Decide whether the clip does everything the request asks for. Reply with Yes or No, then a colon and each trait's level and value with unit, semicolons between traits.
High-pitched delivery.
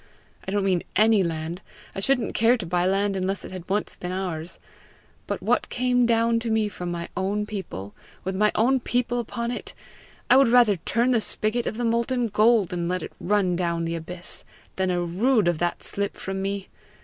Yes: high, 200 Hz